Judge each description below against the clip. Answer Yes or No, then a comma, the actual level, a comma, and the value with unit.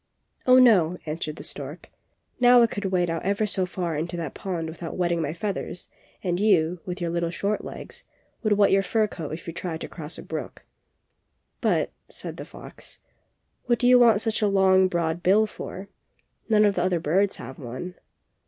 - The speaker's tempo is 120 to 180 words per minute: No, average, 195 wpm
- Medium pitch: Yes, medium, 180 Hz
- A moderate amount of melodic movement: Yes, average, 3.5 semitones